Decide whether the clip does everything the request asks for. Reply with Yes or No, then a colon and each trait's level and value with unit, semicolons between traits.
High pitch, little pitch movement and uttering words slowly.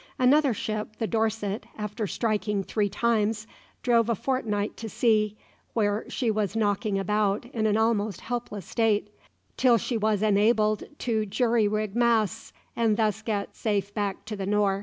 No: high, 215 Hz; narrow, 1.7 semitones; average, 160 wpm